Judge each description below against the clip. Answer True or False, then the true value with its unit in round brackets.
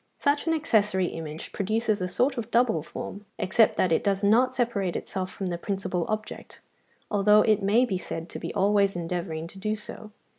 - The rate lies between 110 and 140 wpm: False (190 wpm)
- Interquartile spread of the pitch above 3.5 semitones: False (3.2 semitones)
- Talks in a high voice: True (200 Hz)